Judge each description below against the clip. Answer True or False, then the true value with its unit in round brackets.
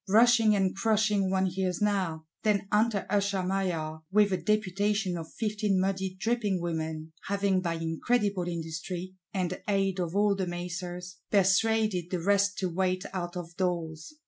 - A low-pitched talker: False (190 Hz)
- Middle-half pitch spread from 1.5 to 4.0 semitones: True (2.6 semitones)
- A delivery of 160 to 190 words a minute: False (145 wpm)